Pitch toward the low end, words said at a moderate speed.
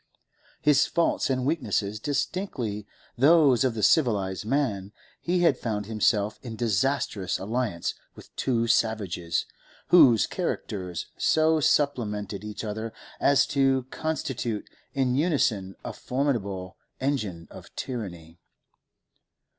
No: low, 115 Hz; slow, 105 wpm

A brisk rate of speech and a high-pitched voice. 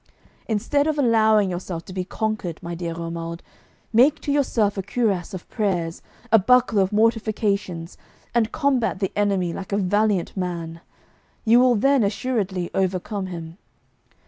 No: average, 145 wpm; high, 200 Hz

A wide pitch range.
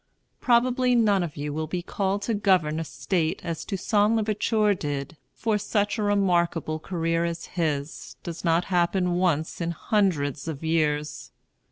No: average, 4.3 semitones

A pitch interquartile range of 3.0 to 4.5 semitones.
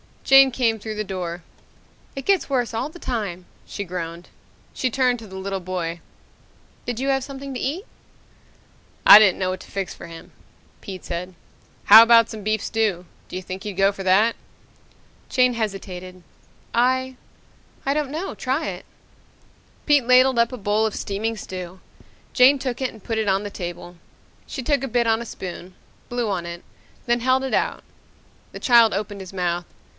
No: average, 5.2 semitones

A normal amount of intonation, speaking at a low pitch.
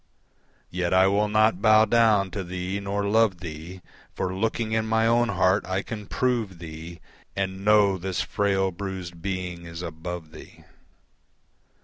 Yes: average, 3.0 semitones; very low, 95 Hz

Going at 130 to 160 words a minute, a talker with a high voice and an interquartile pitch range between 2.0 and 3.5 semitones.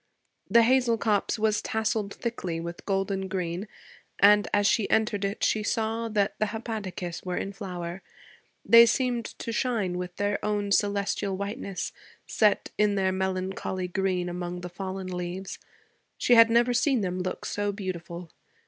Yes: average, 155 wpm; high, 200 Hz; average, 3.0 semitones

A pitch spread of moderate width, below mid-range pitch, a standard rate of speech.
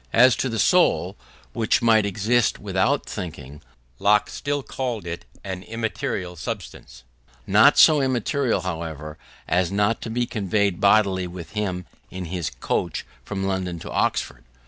Yes: average, 4.1 semitones; low, 100 Hz; average, 145 wpm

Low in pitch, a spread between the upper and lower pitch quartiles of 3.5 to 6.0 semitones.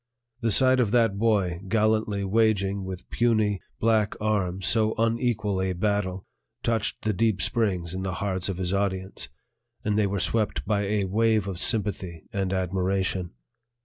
No: low, 100 Hz; average, 2.7 semitones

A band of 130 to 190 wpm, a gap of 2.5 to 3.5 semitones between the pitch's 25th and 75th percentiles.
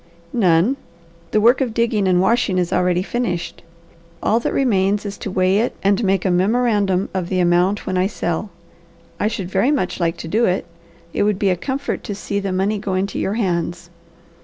No: average, 200 wpm; average, 2.9 semitones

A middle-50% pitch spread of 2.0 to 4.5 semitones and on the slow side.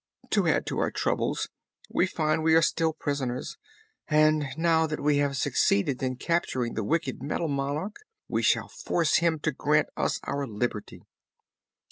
No: average, 2.9 semitones; average, 160 wpm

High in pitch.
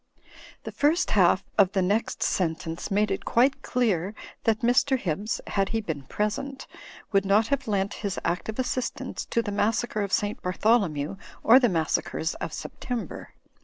Yes: high, 210 Hz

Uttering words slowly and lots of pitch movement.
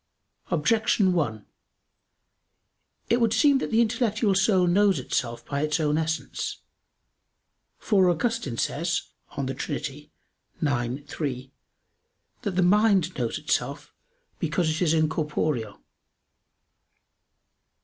Yes: slow, 105 wpm; wide, 5.9 semitones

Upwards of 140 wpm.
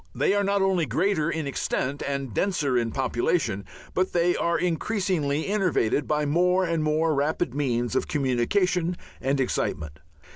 Yes: average, 150 wpm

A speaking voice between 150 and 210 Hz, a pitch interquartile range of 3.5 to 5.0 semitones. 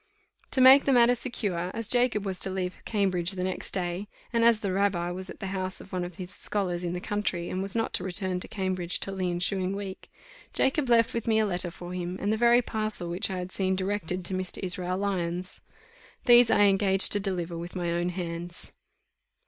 No: high, 190 Hz; narrow, 2.6 semitones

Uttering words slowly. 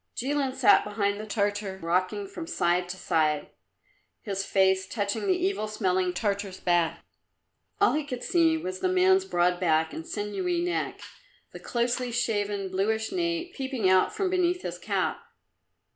No: average, 155 wpm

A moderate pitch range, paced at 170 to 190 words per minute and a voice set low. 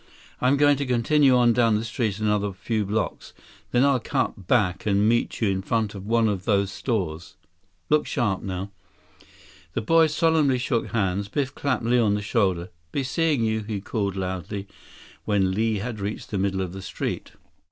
Yes: average, 4.0 semitones; average, 185 wpm; low, 110 Hz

